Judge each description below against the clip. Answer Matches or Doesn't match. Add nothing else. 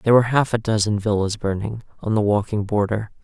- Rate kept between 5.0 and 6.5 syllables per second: Matches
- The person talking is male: Matches